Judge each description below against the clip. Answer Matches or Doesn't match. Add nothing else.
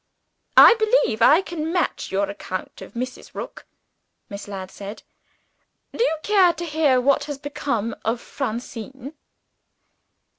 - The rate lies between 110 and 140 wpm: Matches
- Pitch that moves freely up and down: Matches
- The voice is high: Matches